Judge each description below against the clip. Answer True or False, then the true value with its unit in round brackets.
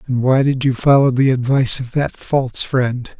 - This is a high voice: False (130 Hz)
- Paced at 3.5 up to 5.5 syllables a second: True (4.9 syllables/s)